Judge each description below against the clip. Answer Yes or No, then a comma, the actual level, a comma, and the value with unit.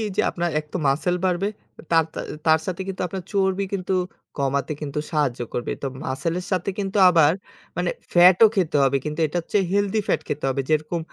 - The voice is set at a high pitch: No, medium, 170 Hz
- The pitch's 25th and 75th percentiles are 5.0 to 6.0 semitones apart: No, average, 4.0 semitones